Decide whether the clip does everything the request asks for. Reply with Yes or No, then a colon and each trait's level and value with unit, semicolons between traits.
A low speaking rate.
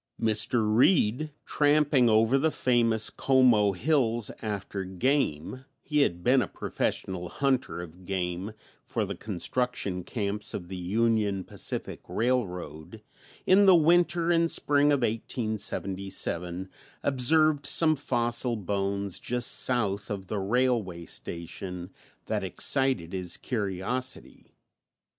Yes: slow, 115 wpm